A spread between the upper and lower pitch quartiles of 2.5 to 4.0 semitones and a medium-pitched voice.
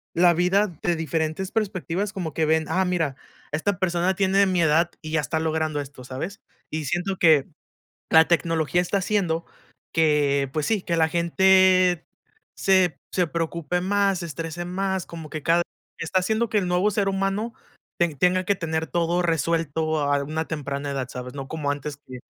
Yes: average, 3.0 semitones; medium, 170 Hz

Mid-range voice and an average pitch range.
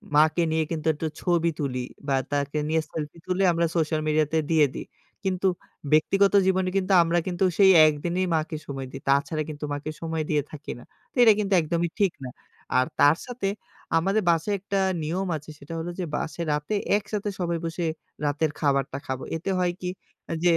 Yes: medium, 160 Hz; average, 3.5 semitones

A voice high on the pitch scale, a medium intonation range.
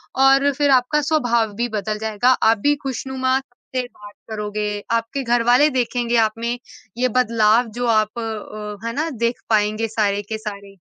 Yes: high, 235 Hz; average, 3.0 semitones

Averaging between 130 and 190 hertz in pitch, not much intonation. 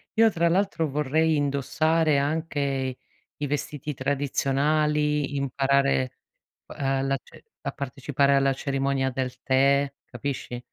Yes: medium, 140 Hz; narrow, 1.8 semitones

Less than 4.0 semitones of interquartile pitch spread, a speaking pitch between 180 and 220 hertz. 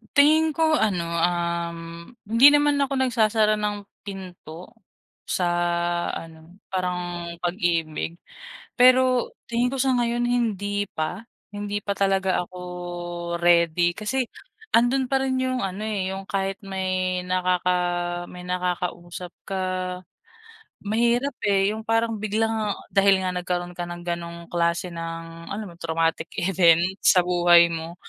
No: average, 4.3 semitones; high, 190 Hz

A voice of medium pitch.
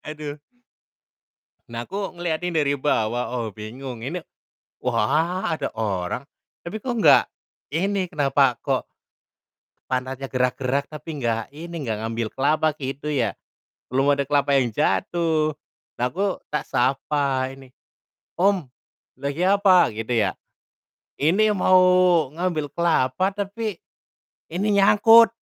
Yes: medium, 145 Hz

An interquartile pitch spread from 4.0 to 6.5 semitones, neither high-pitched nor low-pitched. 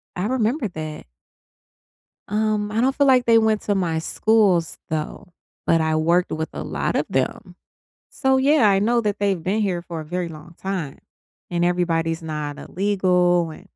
Yes: average, 4.7 semitones; medium, 180 Hz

